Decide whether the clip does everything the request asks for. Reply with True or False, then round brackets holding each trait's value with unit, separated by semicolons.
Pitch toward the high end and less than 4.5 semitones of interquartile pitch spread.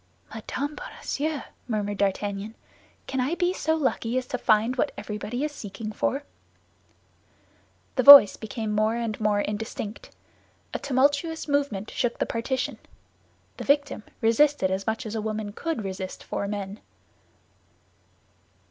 False (225 Hz; 5.2 semitones)